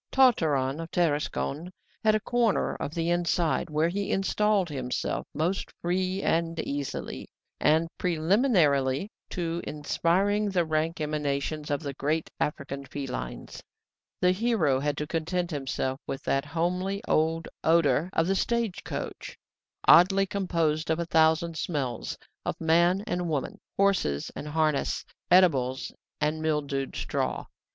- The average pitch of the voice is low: No, medium, 165 Hz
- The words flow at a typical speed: No, slow, 130 wpm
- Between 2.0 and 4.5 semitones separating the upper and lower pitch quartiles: Yes, average, 3.8 semitones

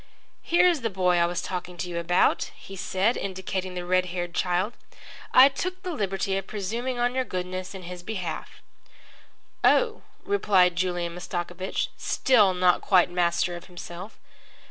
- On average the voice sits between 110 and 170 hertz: No, medium, 185 Hz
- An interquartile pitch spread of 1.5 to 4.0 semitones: Yes, average, 3.3 semitones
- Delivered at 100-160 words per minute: Yes, average, 155 wpm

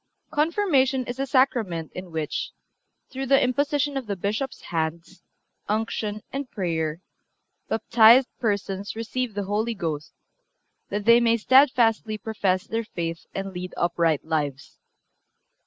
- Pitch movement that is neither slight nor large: No, wide, 6.2 semitones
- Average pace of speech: No, slow, 125 wpm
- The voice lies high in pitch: Yes, high, 215 Hz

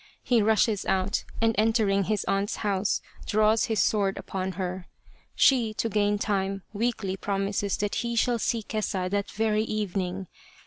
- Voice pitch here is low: No, high, 205 Hz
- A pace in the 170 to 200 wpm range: No, average, 155 wpm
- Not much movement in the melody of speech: Yes, narrow, 2.2 semitones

